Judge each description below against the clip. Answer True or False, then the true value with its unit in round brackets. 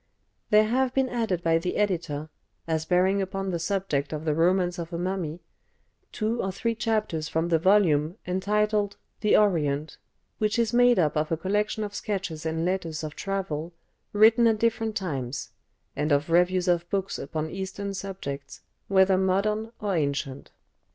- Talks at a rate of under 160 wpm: False (165 wpm)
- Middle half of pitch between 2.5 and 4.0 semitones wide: False (4.5 semitones)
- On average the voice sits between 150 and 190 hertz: True (185 Hz)